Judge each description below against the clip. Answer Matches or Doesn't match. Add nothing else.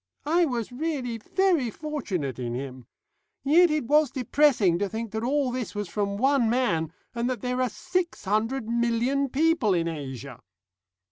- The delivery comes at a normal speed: Matches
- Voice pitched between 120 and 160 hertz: Doesn't match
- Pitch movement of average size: Doesn't match